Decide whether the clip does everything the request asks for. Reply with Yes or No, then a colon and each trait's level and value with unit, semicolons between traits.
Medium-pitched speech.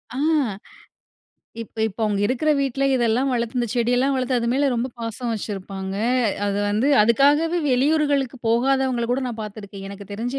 No: high, 240 Hz